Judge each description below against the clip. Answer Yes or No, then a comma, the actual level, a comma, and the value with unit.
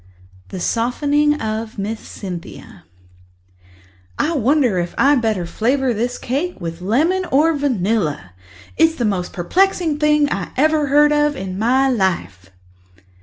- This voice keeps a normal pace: No, slow, 130 wpm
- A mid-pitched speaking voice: No, high, 245 Hz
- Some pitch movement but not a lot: No, wide, 7.3 semitones